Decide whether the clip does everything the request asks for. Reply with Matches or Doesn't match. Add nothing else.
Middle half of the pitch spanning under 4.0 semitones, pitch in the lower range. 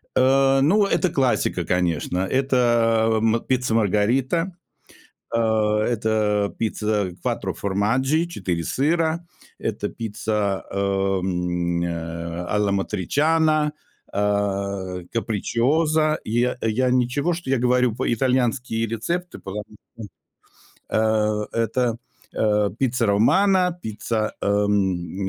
Doesn't match